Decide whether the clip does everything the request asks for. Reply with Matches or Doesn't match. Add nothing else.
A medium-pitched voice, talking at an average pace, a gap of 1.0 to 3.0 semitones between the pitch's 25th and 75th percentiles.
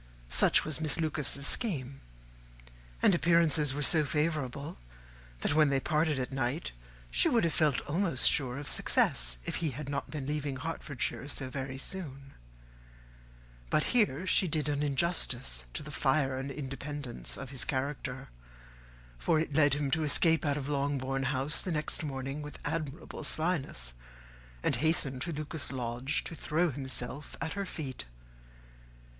Matches